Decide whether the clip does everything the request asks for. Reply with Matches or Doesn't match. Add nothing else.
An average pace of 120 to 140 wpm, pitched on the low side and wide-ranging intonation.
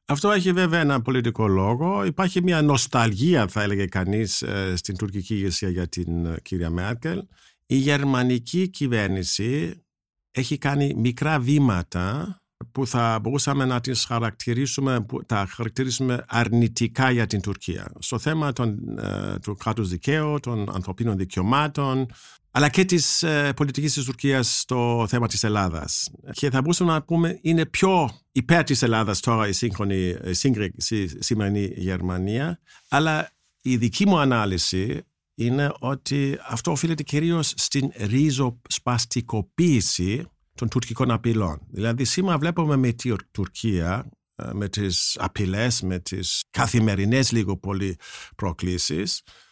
Matches